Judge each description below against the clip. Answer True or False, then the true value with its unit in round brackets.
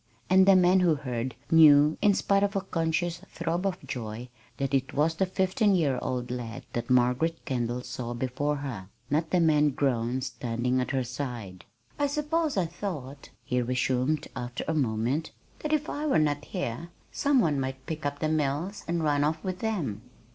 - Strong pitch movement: True (5.7 semitones)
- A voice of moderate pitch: True (145 Hz)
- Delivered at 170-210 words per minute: True (185 wpm)